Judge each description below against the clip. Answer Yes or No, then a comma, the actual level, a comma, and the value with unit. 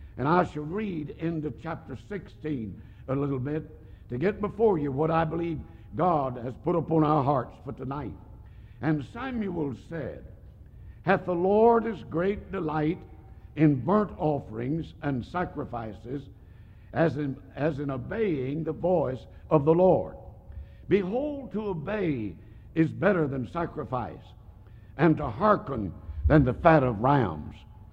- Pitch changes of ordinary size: No, wide, 7.2 semitones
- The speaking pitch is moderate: Yes, medium, 145 Hz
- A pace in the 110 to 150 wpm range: Yes, average, 140 wpm